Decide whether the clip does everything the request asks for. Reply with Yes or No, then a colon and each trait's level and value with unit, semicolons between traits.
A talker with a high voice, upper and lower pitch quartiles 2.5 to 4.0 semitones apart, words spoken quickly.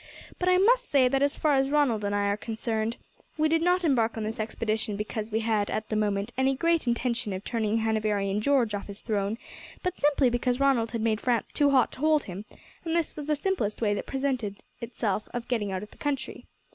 No: high, 230 Hz; average, 4.7 semitones; fast, 225 wpm